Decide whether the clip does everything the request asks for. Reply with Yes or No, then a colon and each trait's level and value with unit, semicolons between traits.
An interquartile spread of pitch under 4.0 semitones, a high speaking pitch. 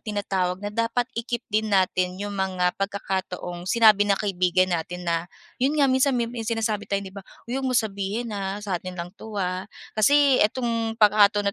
Yes: average, 3.6 semitones; high, 205 Hz